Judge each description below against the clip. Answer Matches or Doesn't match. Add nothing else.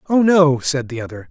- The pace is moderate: Doesn't match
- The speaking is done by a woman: Doesn't match